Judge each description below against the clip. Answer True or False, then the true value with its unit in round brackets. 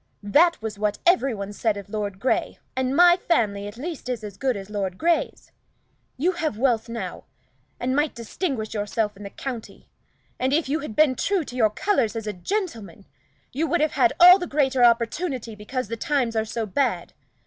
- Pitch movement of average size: False (6.2 semitones)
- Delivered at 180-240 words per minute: True (195 wpm)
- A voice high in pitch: True (245 Hz)